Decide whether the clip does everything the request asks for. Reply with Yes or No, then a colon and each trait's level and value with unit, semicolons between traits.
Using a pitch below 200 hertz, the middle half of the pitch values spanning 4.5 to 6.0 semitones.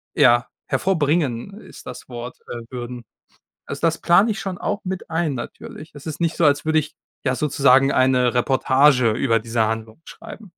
Yes: medium, 140 Hz; average, 5.1 semitones